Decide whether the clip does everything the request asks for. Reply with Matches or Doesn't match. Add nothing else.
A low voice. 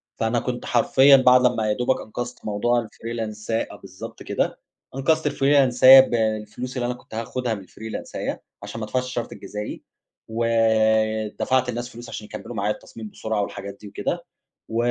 Matches